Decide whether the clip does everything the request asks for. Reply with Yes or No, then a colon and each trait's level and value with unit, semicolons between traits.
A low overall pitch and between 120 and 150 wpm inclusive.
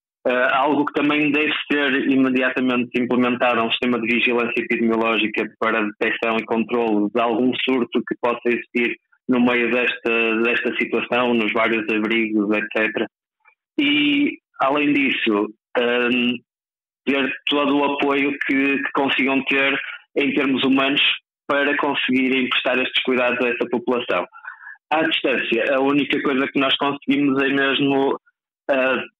Yes: low, 125 Hz; average, 135 wpm